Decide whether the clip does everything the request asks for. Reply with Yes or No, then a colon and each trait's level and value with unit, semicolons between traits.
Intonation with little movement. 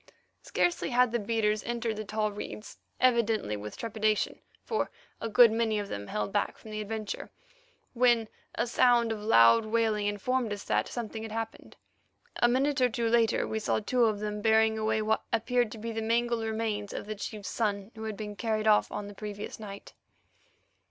Yes: narrow, 1.7 semitones